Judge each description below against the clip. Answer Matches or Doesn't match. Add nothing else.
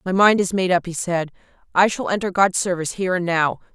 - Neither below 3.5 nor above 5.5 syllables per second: Doesn't match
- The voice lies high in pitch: Doesn't match